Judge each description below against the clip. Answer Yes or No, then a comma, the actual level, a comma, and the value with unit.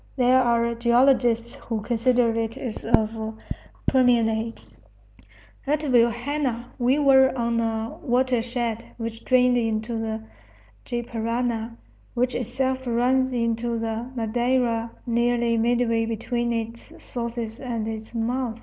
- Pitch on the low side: No, high, 235 Hz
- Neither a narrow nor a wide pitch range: No, narrow, 1.5 semitones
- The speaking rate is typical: No, slow, 120 wpm